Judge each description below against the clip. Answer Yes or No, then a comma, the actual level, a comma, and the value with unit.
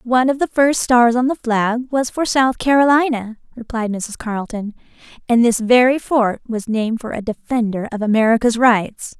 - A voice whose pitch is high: Yes, high, 235 Hz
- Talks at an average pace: Yes, average, 175 wpm